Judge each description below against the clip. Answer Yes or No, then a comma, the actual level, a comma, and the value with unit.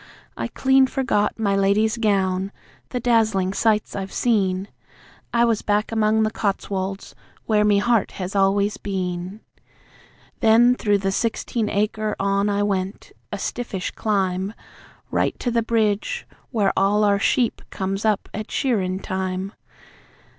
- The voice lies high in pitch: Yes, high, 205 Hz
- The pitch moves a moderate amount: No, narrow, 2.3 semitones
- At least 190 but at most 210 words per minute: No, average, 140 wpm